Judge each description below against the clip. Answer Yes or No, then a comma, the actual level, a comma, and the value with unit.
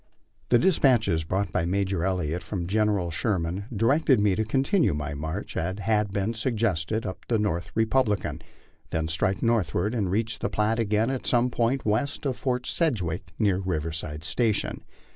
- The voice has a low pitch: Yes, low, 105 Hz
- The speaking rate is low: No, average, 160 wpm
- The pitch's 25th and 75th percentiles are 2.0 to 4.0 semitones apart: No, average, 4.5 semitones